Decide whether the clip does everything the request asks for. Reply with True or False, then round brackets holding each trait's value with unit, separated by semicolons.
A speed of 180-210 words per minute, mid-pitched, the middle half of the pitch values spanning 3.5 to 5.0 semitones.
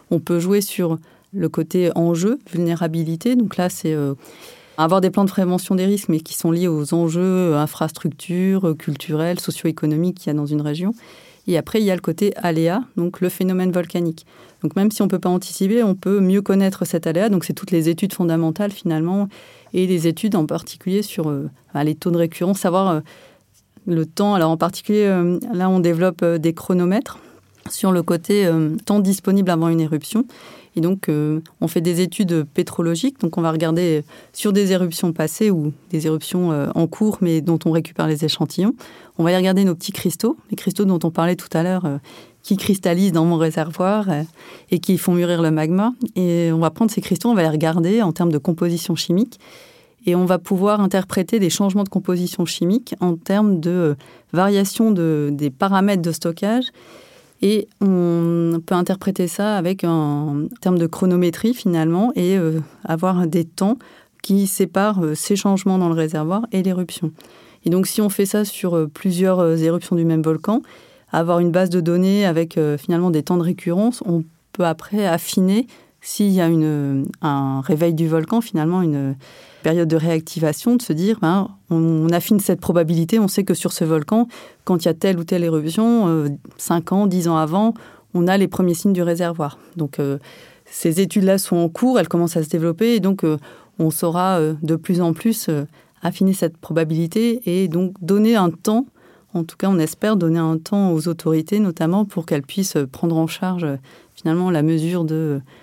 False (190 wpm; 175 Hz; 3.1 semitones)